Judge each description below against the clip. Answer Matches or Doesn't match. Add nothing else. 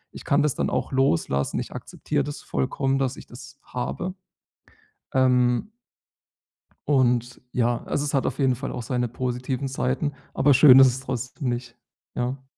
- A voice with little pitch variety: Matches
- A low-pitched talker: Matches